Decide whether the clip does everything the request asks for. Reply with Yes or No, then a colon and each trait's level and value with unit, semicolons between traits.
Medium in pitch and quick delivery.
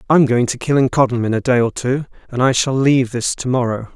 No: low, 125 Hz; fast, 245 wpm